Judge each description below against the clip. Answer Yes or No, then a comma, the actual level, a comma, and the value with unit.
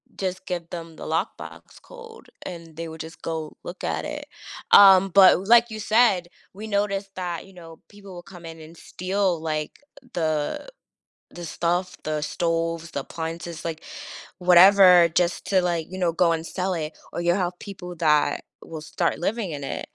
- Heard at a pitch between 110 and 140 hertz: No, medium, 175 Hz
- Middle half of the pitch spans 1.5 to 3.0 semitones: Yes, average, 2.7 semitones